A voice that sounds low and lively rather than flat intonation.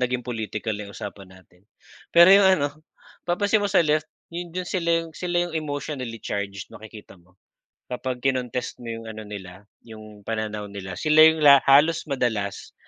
Yes: low, 125 Hz; wide, 7.1 semitones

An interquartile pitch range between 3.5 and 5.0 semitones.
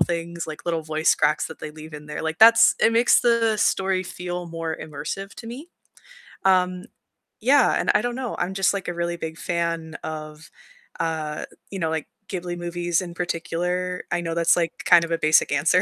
No: narrow, 2.4 semitones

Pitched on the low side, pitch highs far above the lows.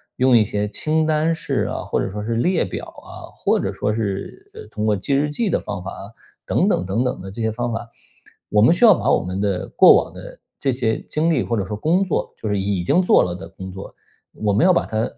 Yes: low, 110 Hz; wide, 7.2 semitones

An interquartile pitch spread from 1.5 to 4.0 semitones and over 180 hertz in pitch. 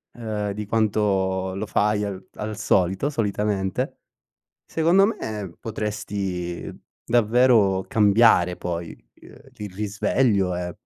No: narrow, 2.4 semitones; low, 105 Hz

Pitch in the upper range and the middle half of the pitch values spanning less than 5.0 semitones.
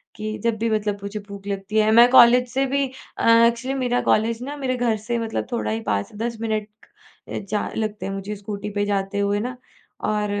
Yes: high, 220 Hz; narrow, 2.5 semitones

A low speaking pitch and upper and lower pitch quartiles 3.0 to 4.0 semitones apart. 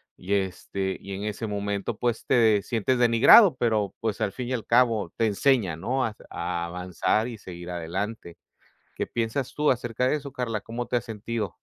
Yes: low, 110 Hz; average, 3.6 semitones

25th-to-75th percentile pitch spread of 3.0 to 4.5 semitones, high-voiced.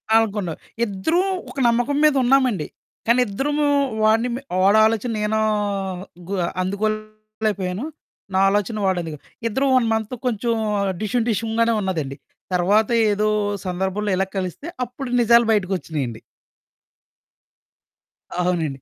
Yes: average, 3.7 semitones; high, 215 Hz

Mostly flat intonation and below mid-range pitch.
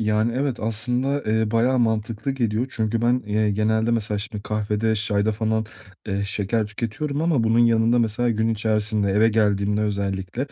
Yes: narrow, 1.9 semitones; low, 110 Hz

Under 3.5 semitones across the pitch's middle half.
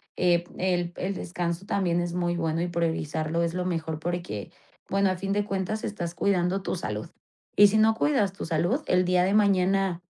Yes: narrow, 2.4 semitones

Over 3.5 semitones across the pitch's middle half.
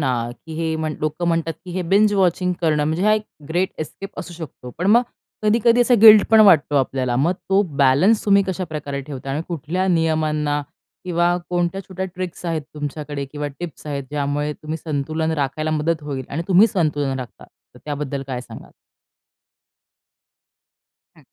Yes: average, 3.9 semitones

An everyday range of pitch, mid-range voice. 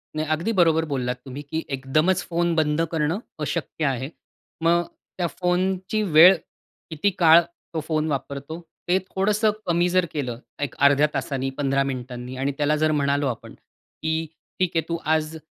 Yes: average, 3.6 semitones; medium, 155 Hz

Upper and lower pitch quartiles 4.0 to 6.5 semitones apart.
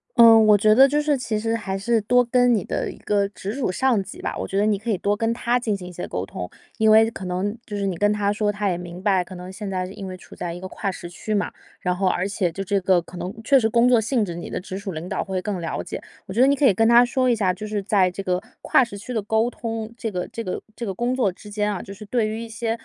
No: average, 3.4 semitones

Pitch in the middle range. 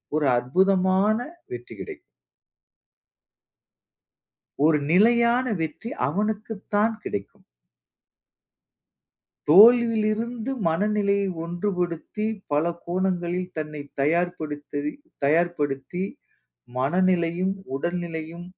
Yes: medium, 180 Hz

